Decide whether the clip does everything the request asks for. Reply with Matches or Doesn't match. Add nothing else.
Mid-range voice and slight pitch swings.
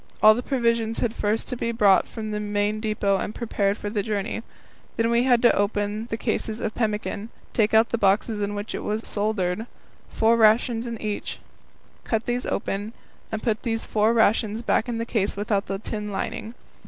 Doesn't match